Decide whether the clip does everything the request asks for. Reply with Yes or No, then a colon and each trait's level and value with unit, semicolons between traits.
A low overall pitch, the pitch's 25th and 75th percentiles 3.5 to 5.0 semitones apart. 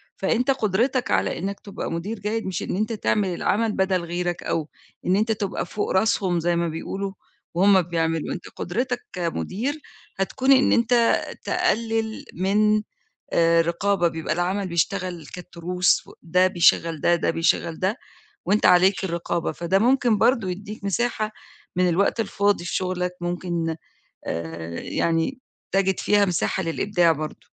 No: medium, 185 Hz; average, 3.8 semitones